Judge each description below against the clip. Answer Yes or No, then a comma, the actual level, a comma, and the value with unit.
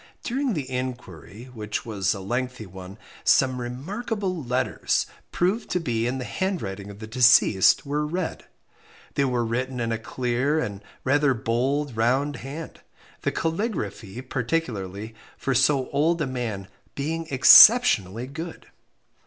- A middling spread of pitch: Yes, average, 4.9 semitones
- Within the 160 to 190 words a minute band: No, slow, 135 wpm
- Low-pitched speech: Yes, low, 130 Hz